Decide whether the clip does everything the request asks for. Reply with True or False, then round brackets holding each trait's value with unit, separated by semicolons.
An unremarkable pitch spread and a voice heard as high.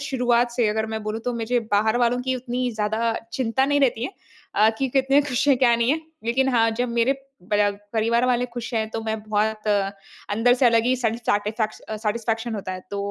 False (2.3 semitones; 235 Hz)